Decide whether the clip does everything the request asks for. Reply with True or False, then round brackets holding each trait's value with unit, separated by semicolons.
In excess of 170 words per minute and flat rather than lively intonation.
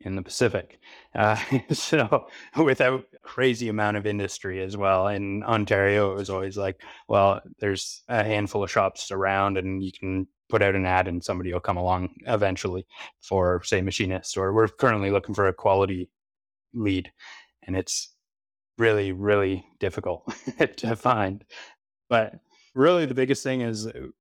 False (155 wpm; 2.2 semitones)